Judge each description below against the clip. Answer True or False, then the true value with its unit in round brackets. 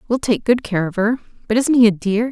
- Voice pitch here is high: True (225 Hz)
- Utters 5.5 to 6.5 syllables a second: True (5.9 syllables/s)